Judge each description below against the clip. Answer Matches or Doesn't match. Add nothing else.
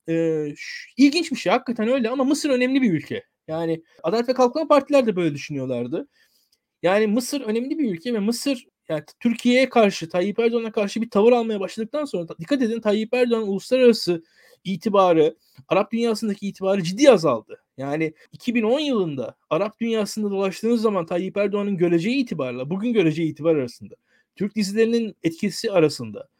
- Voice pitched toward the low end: Doesn't match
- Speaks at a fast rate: Matches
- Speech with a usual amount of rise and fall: Doesn't match